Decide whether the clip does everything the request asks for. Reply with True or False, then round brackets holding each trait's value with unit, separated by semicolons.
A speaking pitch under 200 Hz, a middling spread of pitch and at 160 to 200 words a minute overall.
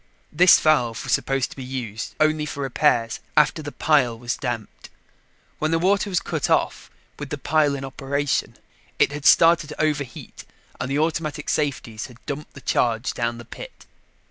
True (140 Hz; 3.8 semitones; 175 wpm)